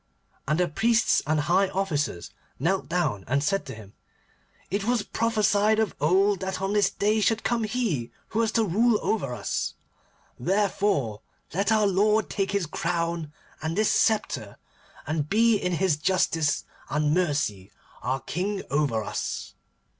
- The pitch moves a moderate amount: No, wide, 5.7 semitones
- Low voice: No, medium, 185 Hz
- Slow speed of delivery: No, average, 155 wpm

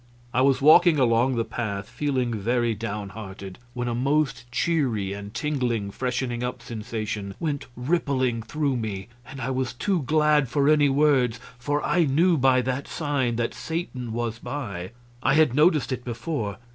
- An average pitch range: Yes, average, 4.1 semitones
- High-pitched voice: No, low, 125 Hz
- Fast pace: No, average, 165 wpm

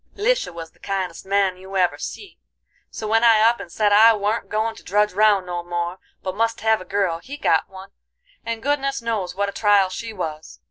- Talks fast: Yes, fast, 215 wpm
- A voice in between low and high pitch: No, high, 205 Hz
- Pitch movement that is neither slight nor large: Yes, average, 3.4 semitones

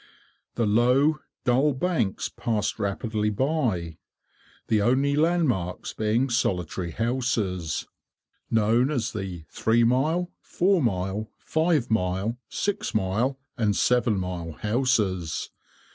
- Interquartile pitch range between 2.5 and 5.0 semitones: No, wide, 5.4 semitones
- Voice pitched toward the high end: No, low, 115 Hz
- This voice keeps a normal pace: No, slow, 110 wpm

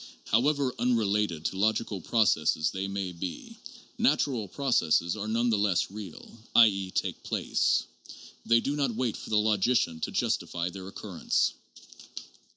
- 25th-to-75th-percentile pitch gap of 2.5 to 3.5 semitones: No, average, 3.9 semitones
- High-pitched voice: No, low, 105 Hz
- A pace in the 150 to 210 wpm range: No, average, 140 wpm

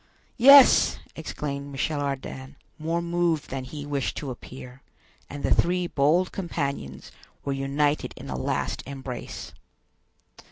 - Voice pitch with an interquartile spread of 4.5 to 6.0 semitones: No, average, 3.6 semitones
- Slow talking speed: Yes, slow, 125 wpm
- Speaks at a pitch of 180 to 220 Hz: No, medium, 145 Hz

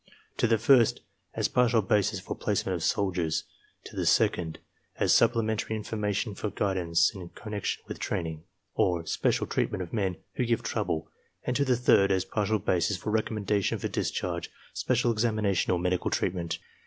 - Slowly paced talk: No, average, 165 wpm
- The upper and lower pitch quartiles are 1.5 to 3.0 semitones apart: No, average, 3.7 semitones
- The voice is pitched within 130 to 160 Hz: No, low, 100 Hz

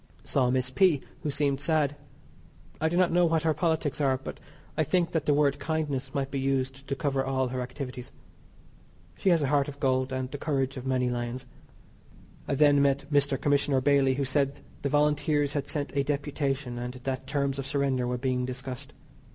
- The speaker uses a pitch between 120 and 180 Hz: Yes, medium, 140 Hz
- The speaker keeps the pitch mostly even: Yes, narrow, 2.0 semitones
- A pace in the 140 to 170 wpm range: No, average, 195 wpm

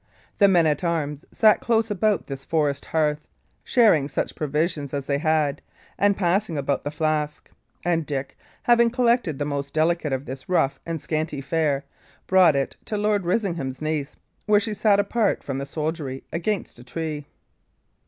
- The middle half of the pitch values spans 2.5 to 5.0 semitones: No, wide, 5.5 semitones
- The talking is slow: No, average, 165 wpm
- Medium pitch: Yes, medium, 155 Hz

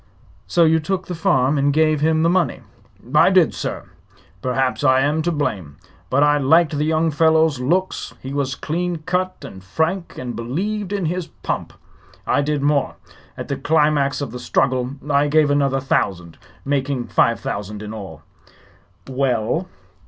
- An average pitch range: Yes, average, 3.7 semitones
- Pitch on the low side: No, medium, 145 Hz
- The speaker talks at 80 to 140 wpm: No, average, 165 wpm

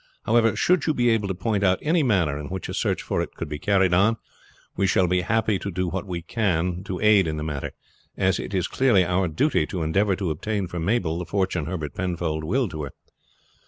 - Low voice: Yes, very low, 95 Hz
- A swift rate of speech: Yes, fast, 235 wpm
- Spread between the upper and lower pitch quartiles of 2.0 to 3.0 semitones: No, average, 3.8 semitones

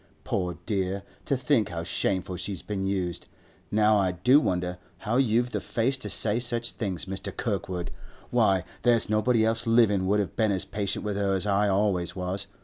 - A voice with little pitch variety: No, average, 3.2 semitones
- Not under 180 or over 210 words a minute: Yes, average, 185 wpm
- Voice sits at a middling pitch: No, low, 100 Hz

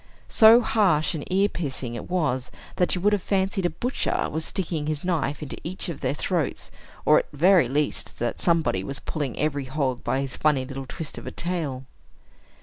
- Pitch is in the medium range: Yes, medium, 155 Hz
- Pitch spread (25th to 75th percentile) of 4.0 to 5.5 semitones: Yes, average, 4.9 semitones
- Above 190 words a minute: Yes, average, 200 wpm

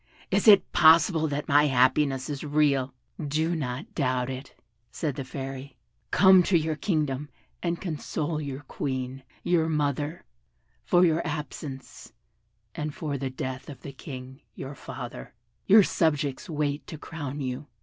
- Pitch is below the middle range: No, medium, 145 Hz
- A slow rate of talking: No, average, 145 wpm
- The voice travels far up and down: No, average, 3.0 semitones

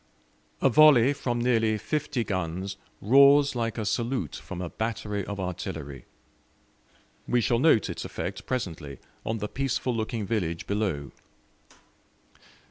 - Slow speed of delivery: Yes, slow, 125 wpm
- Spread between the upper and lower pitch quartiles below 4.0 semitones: No, average, 4.7 semitones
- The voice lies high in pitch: No, low, 110 Hz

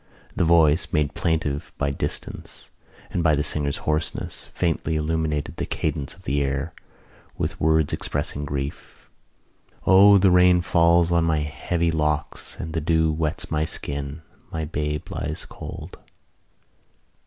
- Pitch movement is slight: Yes, narrow, 2.2 semitones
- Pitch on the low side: Yes, very low, 80 Hz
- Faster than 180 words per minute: No, average, 140 wpm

